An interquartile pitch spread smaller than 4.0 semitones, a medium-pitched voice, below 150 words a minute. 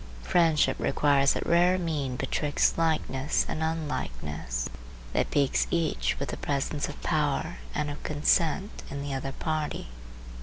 Yes: average, 2.8 semitones; medium, 145 Hz; average, 140 wpm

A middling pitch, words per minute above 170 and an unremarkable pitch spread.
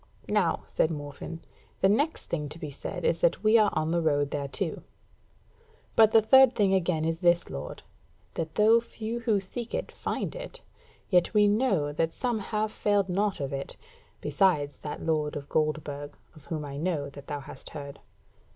No: medium, 170 Hz; average, 180 wpm; wide, 6.4 semitones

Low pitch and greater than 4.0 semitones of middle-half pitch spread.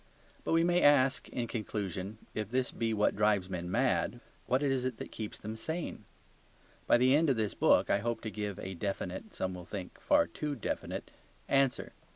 Yes: low, 110 Hz; average, 4.7 semitones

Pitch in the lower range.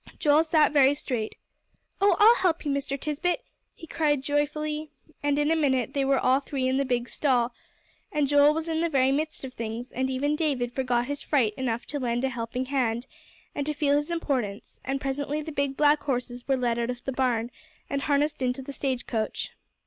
No: very high, 275 Hz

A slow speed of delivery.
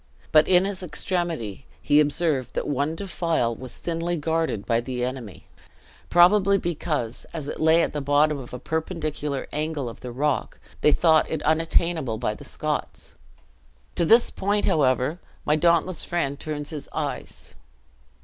No: average, 155 wpm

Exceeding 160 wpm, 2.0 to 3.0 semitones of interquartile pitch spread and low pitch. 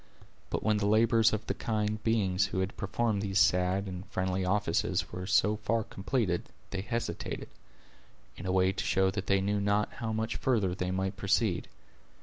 Yes: average, 180 wpm; narrow, 2.4 semitones; low, 100 Hz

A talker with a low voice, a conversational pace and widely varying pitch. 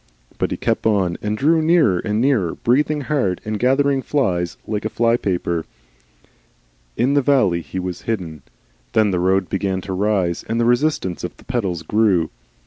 Yes: low, 105 Hz; average, 170 wpm; wide, 5.8 semitones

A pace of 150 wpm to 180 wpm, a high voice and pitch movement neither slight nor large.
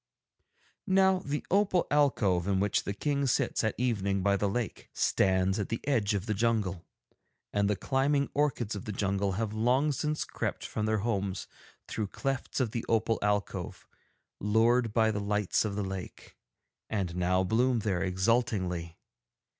No: average, 160 wpm; low, 105 Hz; average, 4.0 semitones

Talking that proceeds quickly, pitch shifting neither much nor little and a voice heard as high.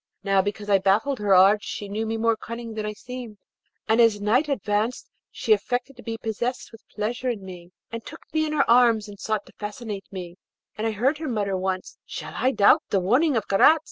Yes: fast, 220 wpm; average, 3.2 semitones; high, 220 Hz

